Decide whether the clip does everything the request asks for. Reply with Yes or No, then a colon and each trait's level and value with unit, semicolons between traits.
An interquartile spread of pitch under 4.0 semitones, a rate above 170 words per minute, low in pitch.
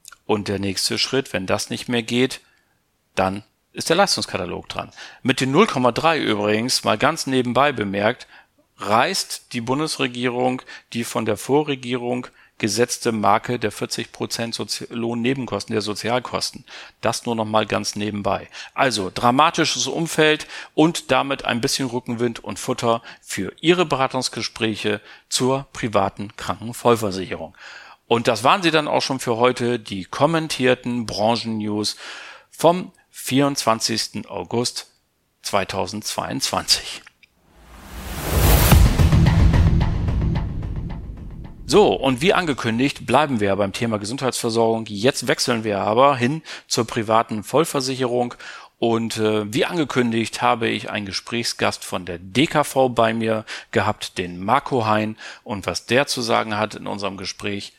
No: average, 3.6 semitones; slow, 125 wpm; low, 115 Hz